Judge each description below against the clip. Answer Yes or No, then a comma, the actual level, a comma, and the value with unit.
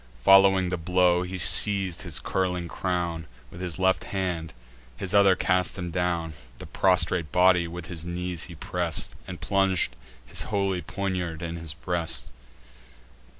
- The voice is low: Yes, very low, 90 Hz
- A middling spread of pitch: No, narrow, 1.8 semitones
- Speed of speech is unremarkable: Yes, average, 150 wpm